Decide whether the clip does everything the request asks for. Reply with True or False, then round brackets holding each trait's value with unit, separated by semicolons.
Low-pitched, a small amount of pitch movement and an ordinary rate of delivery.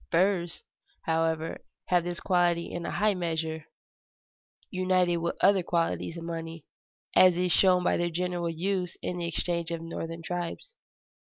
False (175 Hz; 1.5 semitones; 150 wpm)